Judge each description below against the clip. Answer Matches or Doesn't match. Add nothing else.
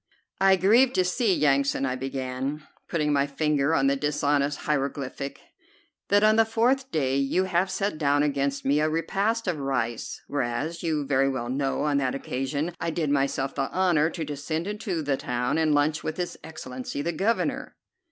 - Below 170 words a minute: Doesn't match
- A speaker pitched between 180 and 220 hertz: Doesn't match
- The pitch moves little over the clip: Doesn't match